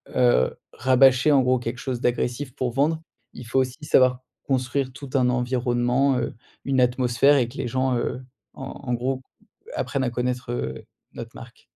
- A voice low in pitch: Yes, low, 130 Hz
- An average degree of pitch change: No, narrow, 1.5 semitones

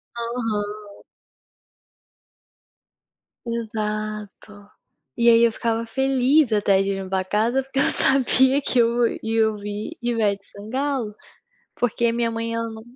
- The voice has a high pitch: Yes, high, 225 Hz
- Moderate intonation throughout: No, narrow, 2.3 semitones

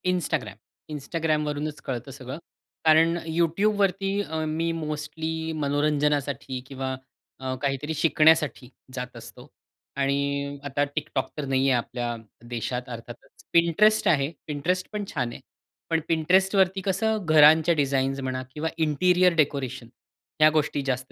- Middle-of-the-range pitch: Yes, medium, 150 Hz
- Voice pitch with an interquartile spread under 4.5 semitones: Yes, average, 3.4 semitones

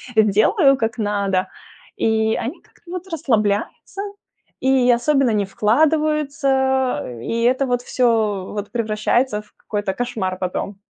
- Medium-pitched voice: No, high, 230 Hz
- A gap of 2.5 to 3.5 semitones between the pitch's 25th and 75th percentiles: No, average, 4.2 semitones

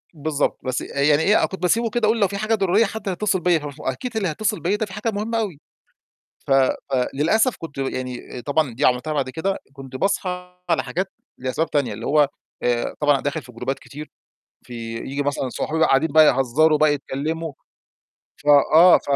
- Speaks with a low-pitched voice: No, medium, 155 Hz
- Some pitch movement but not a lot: No, wide, 5.9 semitones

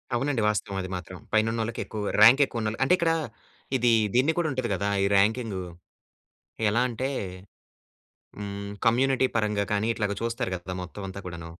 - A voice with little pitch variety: No, average, 3.5 semitones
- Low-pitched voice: Yes, low, 110 Hz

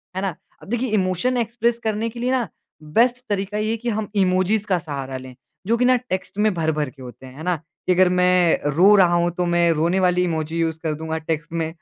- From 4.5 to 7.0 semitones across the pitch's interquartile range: Yes, average, 5.0 semitones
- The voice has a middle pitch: Yes, medium, 180 Hz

